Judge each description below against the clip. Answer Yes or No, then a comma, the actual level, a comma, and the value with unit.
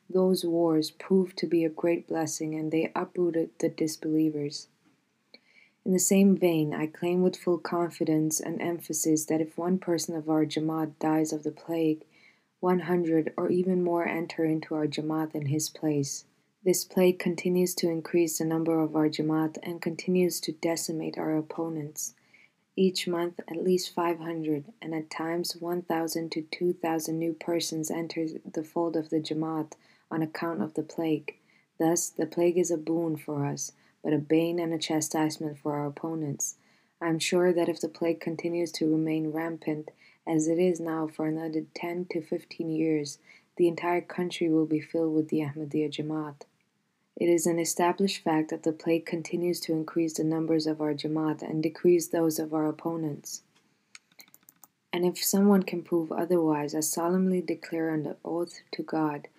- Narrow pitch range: Yes, narrow, 1.8 semitones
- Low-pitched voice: No, medium, 165 Hz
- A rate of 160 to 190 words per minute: Yes, average, 175 wpm